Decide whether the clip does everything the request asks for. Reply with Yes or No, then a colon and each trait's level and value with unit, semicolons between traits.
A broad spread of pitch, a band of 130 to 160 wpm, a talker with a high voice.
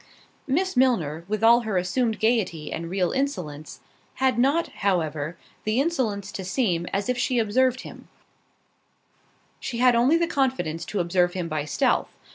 Yes: wide, 6.5 semitones; average, 155 wpm; high, 215 Hz